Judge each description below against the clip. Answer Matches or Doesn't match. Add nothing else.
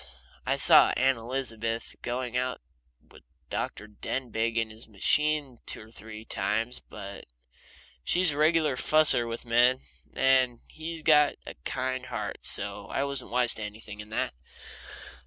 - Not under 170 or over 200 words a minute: Doesn't match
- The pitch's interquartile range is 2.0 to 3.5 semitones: Matches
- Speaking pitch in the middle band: Doesn't match